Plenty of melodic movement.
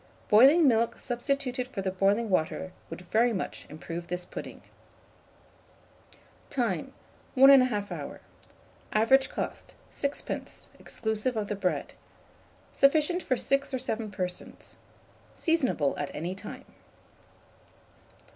Yes: wide, 5.9 semitones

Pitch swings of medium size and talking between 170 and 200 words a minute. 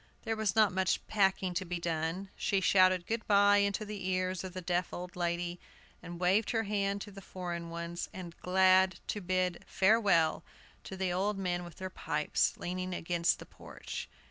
No: narrow, 2.1 semitones; average, 185 wpm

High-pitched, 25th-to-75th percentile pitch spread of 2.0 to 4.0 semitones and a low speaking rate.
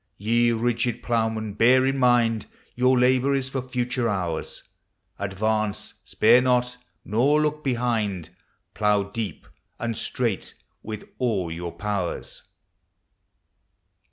No: low, 115 Hz; average, 3.1 semitones; slow, 115 wpm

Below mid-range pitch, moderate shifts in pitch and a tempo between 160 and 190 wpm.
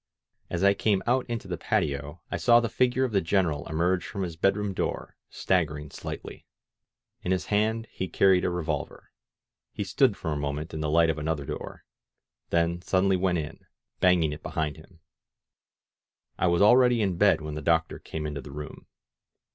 Yes: very low, 90 Hz; average, 4.2 semitones; average, 185 wpm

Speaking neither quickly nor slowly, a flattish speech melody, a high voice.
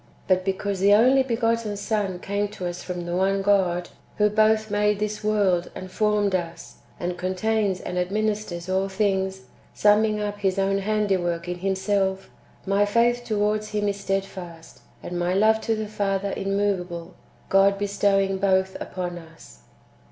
Yes: average, 160 wpm; narrow, 2.0 semitones; high, 195 Hz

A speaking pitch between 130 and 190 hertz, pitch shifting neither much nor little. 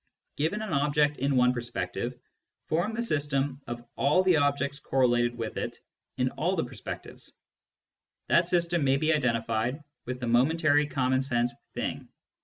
Yes: medium, 140 Hz; average, 3.8 semitones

